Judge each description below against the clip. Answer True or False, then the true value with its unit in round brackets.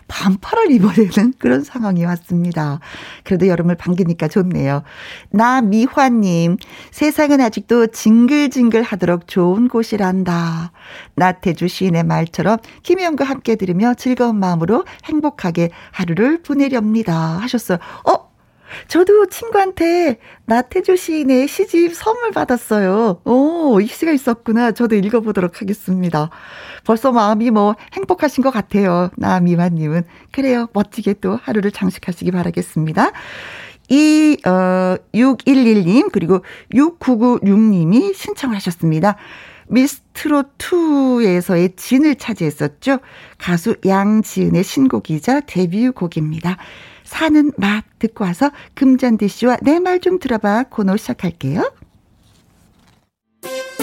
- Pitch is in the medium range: False (220 Hz)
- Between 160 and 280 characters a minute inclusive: True (270 characters per minute)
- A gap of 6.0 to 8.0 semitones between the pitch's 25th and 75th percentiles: True (6.6 semitones)